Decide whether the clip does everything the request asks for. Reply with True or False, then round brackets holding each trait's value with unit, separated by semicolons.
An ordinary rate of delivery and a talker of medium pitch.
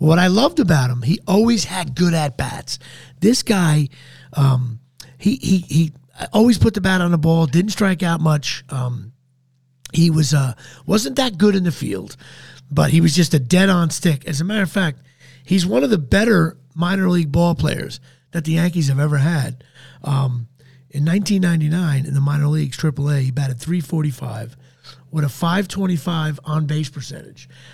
True (180 wpm; 155 Hz)